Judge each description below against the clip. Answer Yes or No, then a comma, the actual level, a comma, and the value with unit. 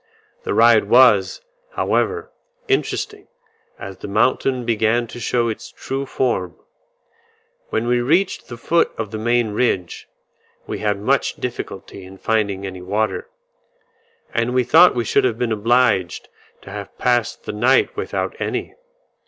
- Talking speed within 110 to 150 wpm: Yes, average, 145 wpm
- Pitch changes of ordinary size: Yes, average, 3.5 semitones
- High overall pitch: No, low, 115 Hz